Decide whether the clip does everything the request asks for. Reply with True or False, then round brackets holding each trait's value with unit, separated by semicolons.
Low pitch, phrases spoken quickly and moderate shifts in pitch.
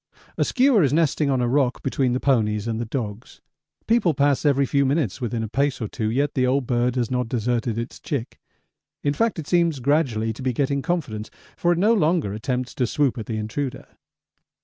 True (130 Hz; 210 wpm; 3.8 semitones)